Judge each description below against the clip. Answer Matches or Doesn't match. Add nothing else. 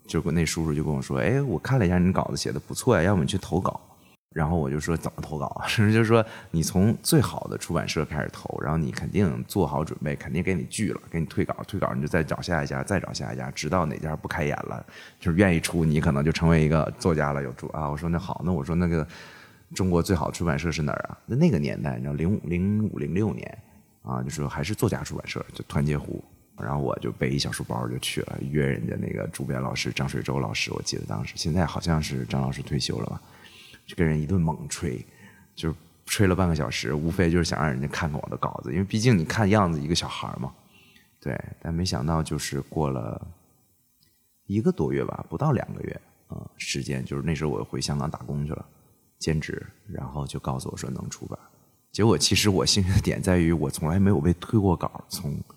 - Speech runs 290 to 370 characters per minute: Matches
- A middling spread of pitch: Matches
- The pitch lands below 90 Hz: Matches